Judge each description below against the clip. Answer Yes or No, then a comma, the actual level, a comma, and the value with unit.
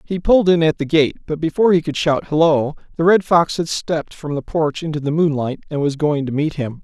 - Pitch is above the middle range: No, medium, 155 Hz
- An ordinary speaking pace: No, fast, 255 wpm